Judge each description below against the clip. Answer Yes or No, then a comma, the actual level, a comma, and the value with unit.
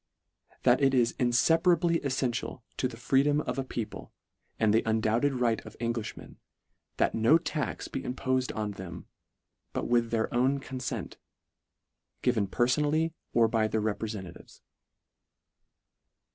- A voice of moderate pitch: No, low, 120 Hz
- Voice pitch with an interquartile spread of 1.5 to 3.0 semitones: No, average, 3.5 semitones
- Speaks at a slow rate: Yes, slow, 130 wpm